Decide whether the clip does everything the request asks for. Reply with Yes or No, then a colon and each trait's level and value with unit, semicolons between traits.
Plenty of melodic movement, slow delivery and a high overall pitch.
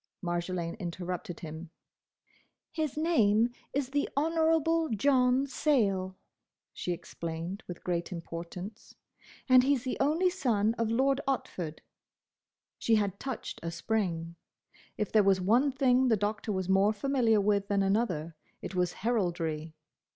Yes: wide, 6.6 semitones; slow, 130 wpm; high, 210 Hz